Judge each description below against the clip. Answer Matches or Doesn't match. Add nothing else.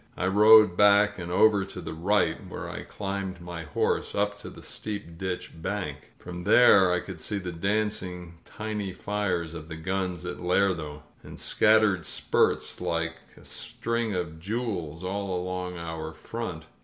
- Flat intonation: Doesn't match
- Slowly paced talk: Doesn't match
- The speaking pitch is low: Matches